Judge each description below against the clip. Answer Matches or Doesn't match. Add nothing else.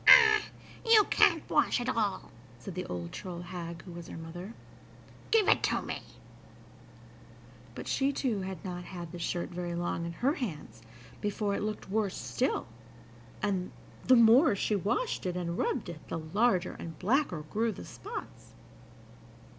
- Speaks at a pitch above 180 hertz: Matches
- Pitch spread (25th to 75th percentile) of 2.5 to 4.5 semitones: Doesn't match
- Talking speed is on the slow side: Doesn't match